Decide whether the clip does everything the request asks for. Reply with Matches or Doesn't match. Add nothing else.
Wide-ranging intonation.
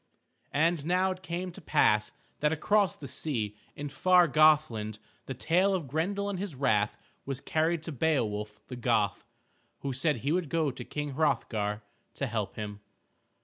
Matches